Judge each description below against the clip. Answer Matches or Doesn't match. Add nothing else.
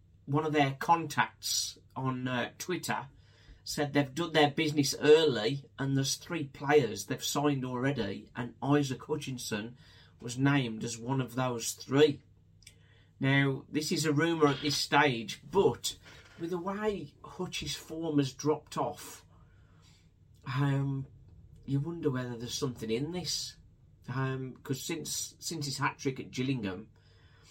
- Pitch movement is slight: Doesn't match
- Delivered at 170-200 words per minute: Doesn't match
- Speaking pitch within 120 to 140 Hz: Matches